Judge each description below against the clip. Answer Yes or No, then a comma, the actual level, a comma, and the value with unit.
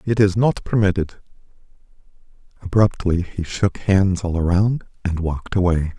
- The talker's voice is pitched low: Yes, very low, 95 Hz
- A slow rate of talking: Yes, slow, 130 wpm